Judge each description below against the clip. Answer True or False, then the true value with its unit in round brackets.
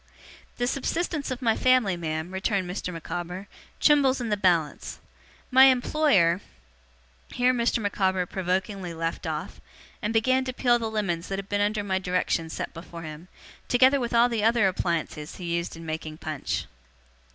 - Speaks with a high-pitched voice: True (195 Hz)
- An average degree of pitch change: False (6.0 semitones)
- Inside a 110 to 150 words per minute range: False (165 wpm)